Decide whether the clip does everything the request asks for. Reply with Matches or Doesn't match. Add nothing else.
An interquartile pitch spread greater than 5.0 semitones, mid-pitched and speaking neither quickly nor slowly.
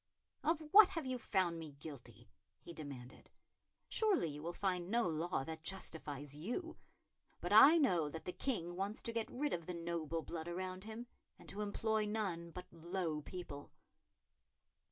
Matches